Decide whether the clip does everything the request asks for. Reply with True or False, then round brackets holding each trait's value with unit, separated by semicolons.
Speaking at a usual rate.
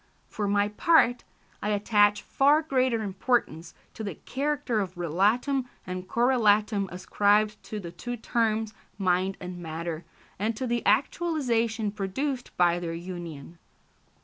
False (130 wpm)